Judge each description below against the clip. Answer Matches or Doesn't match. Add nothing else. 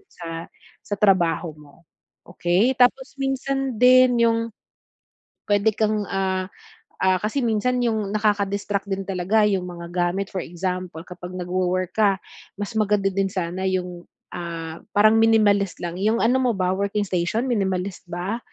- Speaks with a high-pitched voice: Matches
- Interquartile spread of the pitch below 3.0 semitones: Doesn't match